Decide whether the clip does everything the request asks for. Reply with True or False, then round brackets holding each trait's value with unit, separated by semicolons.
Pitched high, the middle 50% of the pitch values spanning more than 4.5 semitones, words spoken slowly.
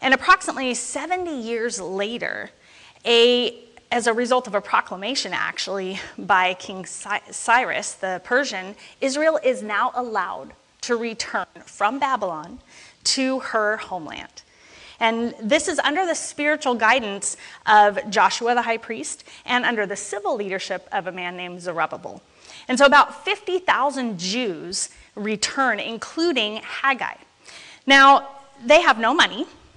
True (240 Hz; 5.0 semitones; 130 wpm)